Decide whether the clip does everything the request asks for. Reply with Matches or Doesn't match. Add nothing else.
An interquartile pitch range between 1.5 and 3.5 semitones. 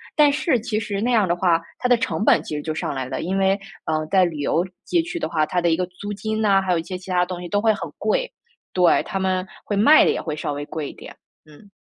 Doesn't match